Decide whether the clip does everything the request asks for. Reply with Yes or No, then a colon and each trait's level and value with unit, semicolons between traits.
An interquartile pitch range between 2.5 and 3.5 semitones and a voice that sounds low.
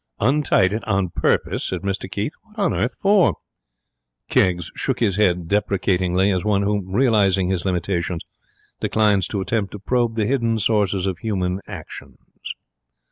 Yes: average, 3.2 semitones; low, 100 Hz